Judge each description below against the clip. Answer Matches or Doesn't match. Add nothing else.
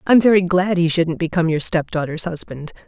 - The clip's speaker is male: Doesn't match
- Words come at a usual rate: Matches